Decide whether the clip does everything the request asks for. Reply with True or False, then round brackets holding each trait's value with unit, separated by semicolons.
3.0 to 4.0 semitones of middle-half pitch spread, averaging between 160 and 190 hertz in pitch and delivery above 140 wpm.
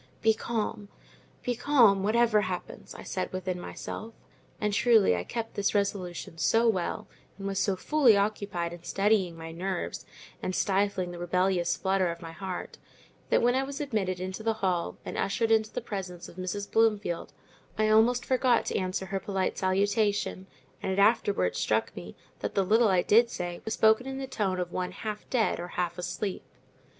False (3.3 semitones; 200 Hz; 180 wpm)